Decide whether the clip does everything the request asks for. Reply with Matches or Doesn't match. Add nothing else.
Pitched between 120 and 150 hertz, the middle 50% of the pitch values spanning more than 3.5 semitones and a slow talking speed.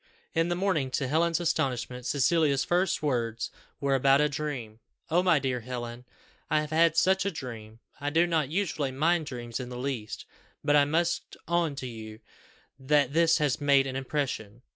Doesn't match